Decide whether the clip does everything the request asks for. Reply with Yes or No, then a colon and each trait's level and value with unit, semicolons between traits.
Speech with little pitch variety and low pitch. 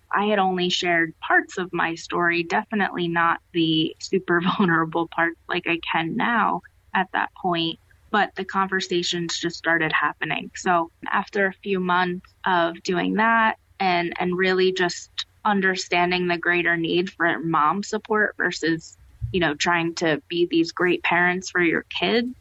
No: narrow, 2.0 semitones; medium, 175 Hz